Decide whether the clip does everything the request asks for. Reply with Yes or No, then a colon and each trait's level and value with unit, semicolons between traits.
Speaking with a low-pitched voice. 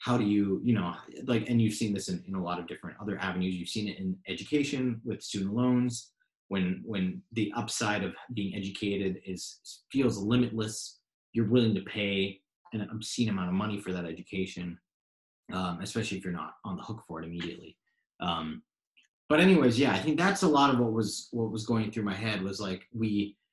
Yes: low, 100 Hz